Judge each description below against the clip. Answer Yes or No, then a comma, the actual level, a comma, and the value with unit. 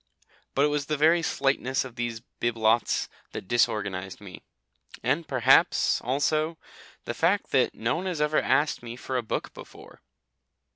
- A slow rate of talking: No, average, 155 wpm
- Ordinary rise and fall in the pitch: Yes, average, 4.6 semitones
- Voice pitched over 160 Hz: No, low, 130 Hz